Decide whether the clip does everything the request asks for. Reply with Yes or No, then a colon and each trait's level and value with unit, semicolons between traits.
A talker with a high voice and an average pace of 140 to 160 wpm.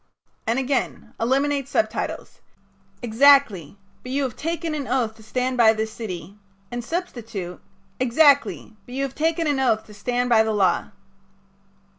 Yes: high, 245 Hz; average, 155 wpm